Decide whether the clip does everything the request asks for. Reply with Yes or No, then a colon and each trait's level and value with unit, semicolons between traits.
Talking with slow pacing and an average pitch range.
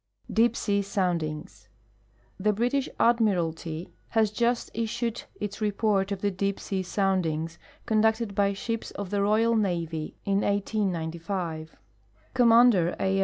Yes: slow, 120 wpm; average, 3.8 semitones